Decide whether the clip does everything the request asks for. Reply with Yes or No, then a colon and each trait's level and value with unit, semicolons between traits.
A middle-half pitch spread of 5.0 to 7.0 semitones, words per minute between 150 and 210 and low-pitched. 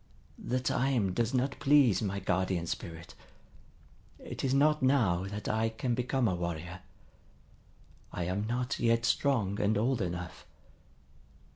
No: wide, 5.5 semitones; slow, 135 wpm; low, 110 Hz